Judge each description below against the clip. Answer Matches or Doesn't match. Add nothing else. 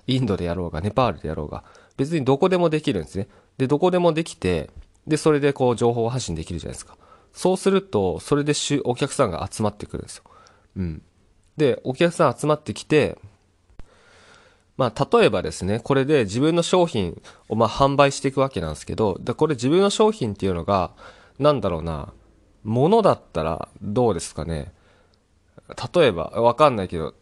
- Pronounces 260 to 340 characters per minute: Doesn't match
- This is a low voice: Matches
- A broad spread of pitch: Matches